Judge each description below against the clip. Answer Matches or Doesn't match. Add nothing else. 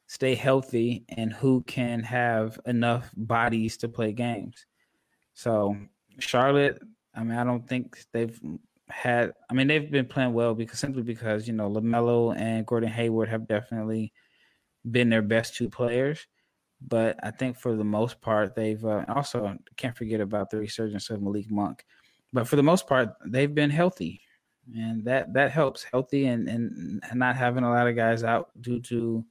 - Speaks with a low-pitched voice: Matches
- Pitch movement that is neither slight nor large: Doesn't match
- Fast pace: Doesn't match